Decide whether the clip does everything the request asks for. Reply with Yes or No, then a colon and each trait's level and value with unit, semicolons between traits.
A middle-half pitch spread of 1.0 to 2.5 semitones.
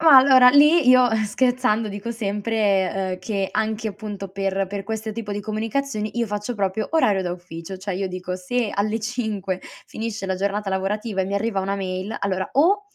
No: average, 2.9 semitones